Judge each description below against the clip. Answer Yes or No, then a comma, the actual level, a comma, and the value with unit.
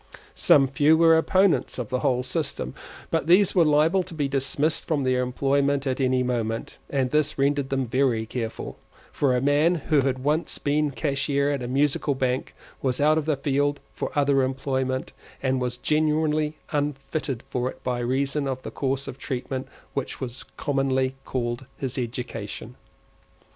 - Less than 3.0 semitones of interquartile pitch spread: Yes, narrow, 2.4 semitones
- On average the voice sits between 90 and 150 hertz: Yes, low, 135 Hz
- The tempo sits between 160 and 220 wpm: Yes, average, 170 wpm